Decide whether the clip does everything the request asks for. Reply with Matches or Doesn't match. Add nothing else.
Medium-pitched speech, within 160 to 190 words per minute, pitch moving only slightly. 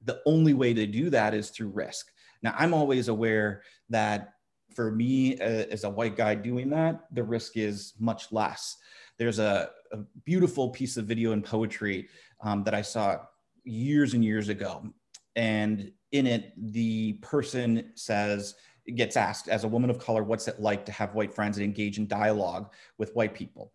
Doesn't match